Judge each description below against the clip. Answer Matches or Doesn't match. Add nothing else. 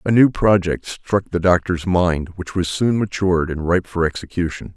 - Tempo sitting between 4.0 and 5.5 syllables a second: Matches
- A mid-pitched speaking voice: Doesn't match